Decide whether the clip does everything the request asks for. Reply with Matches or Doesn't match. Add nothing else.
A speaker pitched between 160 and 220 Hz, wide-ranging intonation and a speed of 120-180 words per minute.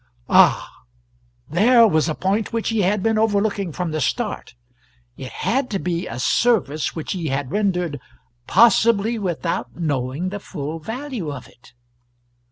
Matches